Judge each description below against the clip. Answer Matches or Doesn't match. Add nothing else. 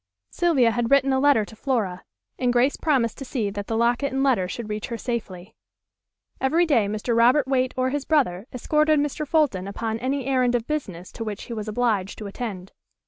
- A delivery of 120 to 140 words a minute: Doesn't match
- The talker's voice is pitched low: Doesn't match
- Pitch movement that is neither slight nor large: Matches